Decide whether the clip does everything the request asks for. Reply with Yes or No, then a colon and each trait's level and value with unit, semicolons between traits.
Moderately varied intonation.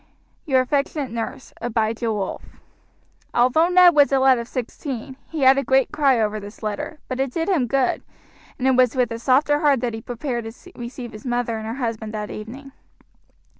Yes: average, 3.3 semitones